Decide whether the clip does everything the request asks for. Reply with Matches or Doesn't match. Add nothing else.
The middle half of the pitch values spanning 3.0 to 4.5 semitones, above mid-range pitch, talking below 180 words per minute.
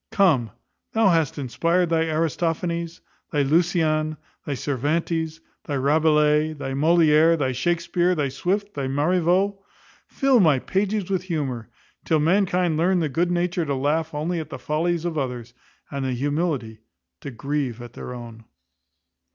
Doesn't match